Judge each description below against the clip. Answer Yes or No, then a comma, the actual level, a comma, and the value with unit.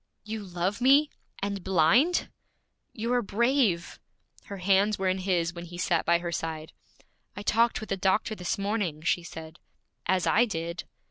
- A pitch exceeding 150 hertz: Yes, high, 190 Hz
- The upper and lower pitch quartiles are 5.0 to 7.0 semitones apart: No, average, 4.0 semitones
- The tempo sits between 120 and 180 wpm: Yes, average, 165 wpm